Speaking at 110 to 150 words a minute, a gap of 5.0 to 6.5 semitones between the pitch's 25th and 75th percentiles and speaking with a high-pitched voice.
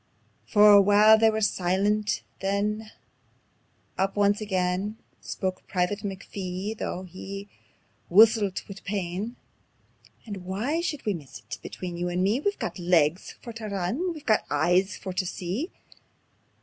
No: average, 140 wpm; average, 2.7 semitones; high, 200 Hz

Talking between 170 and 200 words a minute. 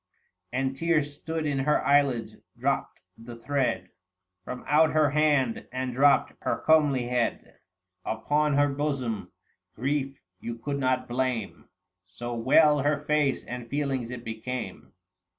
No: slow, 135 wpm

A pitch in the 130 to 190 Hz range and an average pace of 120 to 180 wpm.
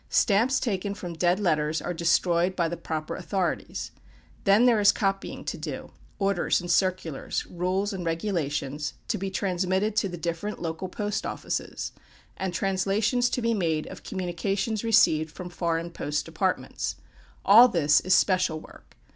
Yes: medium, 185 Hz; average, 155 wpm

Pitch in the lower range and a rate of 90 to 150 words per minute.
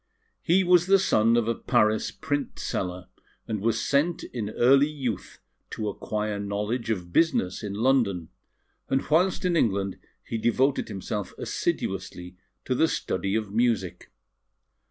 Yes: low, 115 Hz; average, 140 wpm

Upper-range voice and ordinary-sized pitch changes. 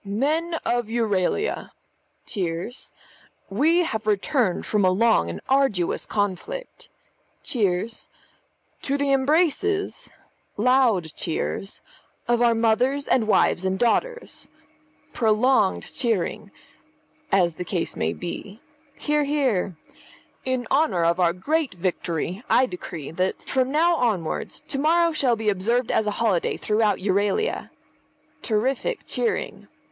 No: high, 225 Hz; wide, 6.4 semitones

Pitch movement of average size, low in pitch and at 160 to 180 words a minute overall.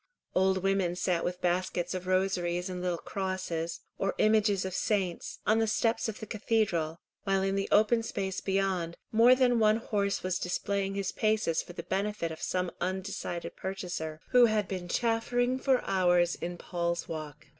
No: average, 3.2 semitones; high, 190 Hz; average, 170 wpm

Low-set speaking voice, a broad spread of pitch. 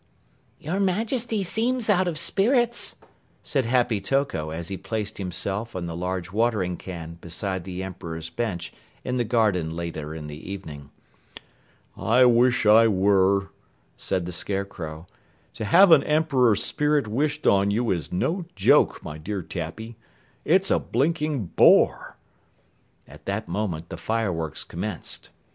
Yes: low, 105 Hz; wide, 7.7 semitones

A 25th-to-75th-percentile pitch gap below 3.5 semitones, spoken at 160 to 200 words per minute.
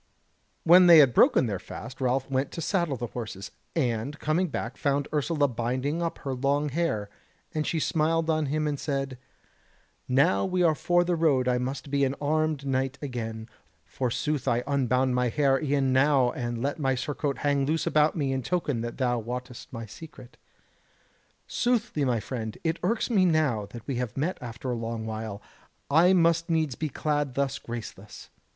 No: average, 4.0 semitones; average, 180 wpm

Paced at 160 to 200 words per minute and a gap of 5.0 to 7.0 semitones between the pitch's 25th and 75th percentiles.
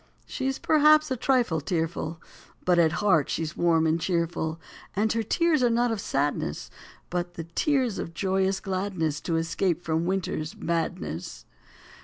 Yes: average, 165 wpm; average, 5.3 semitones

